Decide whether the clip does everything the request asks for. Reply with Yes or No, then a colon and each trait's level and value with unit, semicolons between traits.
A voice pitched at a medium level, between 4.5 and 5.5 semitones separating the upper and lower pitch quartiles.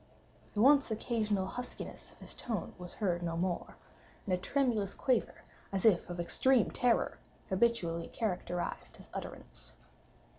No: high, 200 Hz; average, 5.0 semitones